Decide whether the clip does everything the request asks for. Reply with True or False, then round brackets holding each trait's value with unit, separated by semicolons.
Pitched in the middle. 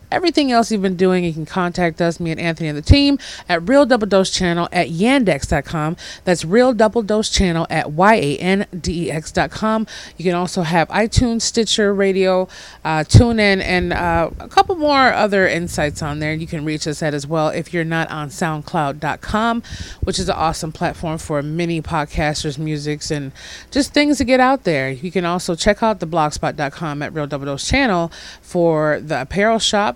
True (175 Hz)